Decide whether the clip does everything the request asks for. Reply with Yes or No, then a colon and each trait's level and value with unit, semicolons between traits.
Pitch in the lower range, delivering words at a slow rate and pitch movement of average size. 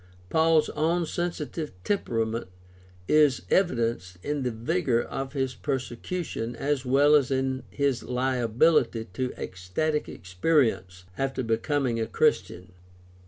Yes: low, 130 Hz; slow, 115 wpm; average, 4.7 semitones